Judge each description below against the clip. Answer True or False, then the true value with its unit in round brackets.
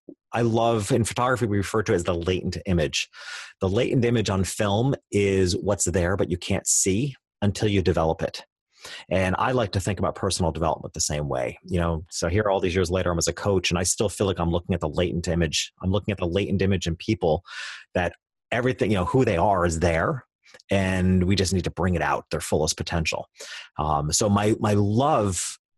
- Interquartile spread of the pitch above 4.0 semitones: False (3.3 semitones)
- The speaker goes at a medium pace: False (220 wpm)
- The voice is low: True (95 Hz)